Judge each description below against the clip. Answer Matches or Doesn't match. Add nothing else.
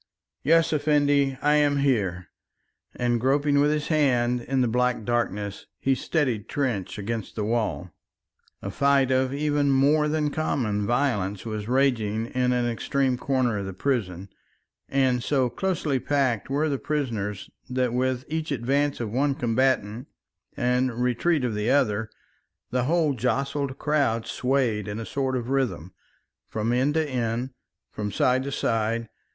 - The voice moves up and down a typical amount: Matches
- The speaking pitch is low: Matches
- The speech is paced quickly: Doesn't match